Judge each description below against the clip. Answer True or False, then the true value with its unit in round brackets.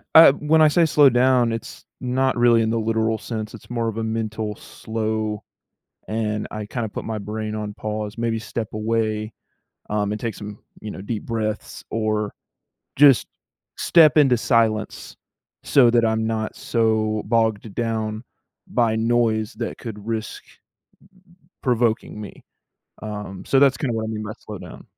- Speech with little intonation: True (1.6 semitones)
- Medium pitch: False (110 Hz)